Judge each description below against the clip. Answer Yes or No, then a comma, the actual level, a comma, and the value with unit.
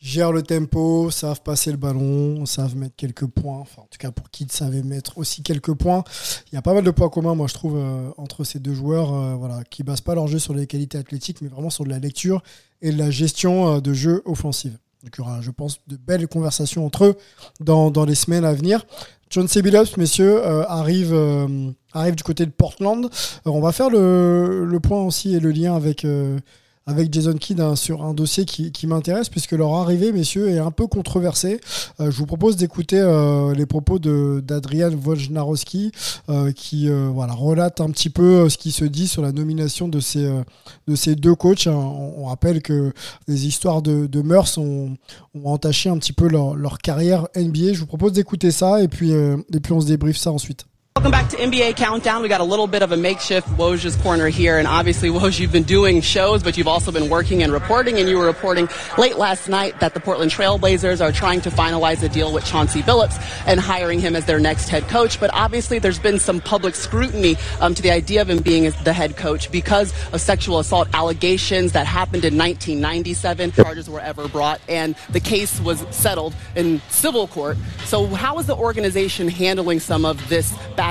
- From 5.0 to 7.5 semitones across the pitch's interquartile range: No, average, 3.8 semitones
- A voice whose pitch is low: No, medium, 160 Hz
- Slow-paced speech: No, average, 215 wpm